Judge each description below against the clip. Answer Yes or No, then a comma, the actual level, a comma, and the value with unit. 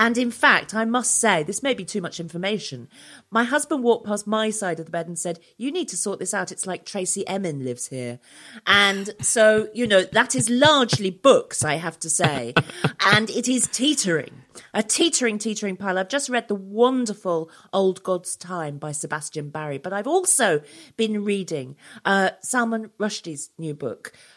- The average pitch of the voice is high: Yes, high, 200 Hz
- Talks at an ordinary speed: Yes, average, 185 wpm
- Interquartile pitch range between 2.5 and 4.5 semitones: No, wide, 5.6 semitones